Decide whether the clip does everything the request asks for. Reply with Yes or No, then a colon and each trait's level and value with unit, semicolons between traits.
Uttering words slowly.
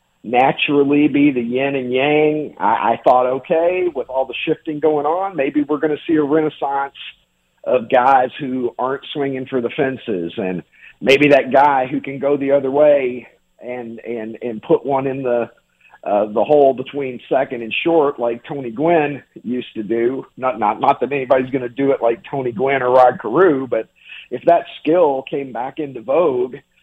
No: average, 190 wpm